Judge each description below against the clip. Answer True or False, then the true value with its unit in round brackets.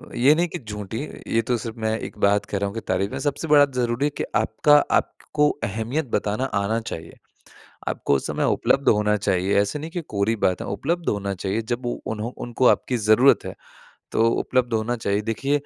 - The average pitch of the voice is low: True (115 Hz)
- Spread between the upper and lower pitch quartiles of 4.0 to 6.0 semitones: True (4.5 semitones)